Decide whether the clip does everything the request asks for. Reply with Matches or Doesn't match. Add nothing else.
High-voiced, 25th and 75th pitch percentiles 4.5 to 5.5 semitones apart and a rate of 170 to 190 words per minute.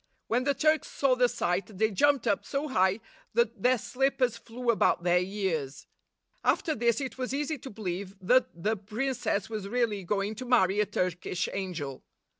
Matches